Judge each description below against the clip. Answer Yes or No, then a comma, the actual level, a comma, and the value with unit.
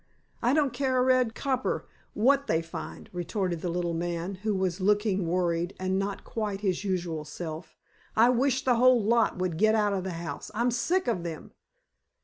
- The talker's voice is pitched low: No, high, 195 Hz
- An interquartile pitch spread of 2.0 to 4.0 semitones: No, average, 5.3 semitones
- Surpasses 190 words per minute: No, average, 185 wpm